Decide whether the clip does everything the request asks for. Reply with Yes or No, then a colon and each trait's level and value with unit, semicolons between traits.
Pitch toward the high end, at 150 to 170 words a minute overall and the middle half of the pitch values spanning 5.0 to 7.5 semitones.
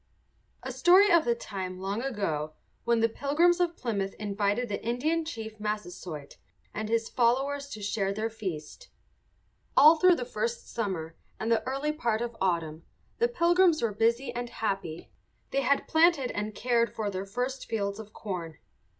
Yes: high, 225 Hz; average, 165 wpm; wide, 5.5 semitones